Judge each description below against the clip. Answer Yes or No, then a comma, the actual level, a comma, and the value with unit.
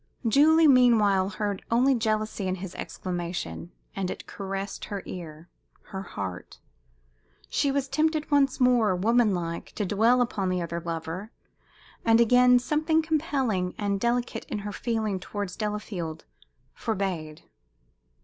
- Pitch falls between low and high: No, high, 210 Hz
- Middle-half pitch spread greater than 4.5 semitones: Yes, average, 5.1 semitones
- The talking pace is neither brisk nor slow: No, slow, 130 wpm